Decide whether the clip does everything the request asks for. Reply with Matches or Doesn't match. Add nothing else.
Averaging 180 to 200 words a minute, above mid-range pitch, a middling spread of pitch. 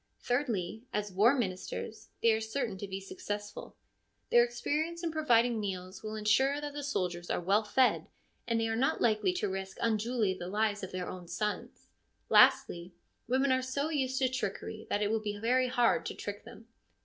Matches